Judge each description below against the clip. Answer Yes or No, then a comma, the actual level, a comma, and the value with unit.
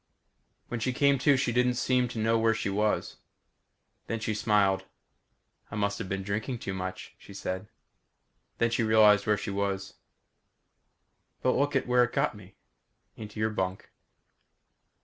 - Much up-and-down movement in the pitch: No, average, 3.3 semitones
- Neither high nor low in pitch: No, low, 110 Hz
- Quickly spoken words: No, average, 155 wpm